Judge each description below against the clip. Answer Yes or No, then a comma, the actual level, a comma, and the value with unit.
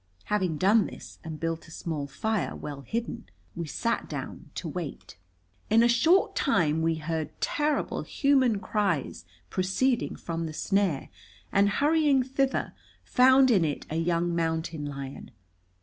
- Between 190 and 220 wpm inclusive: No, average, 145 wpm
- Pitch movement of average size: No, wide, 6.7 semitones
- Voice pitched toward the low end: No, medium, 180 Hz